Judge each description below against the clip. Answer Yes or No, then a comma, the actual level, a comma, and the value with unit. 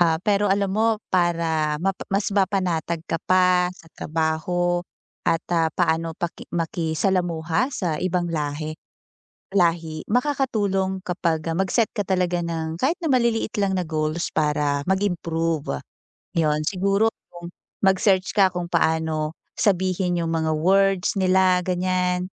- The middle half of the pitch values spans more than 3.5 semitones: No, average, 2.9 semitones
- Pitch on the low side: No, medium, 175 Hz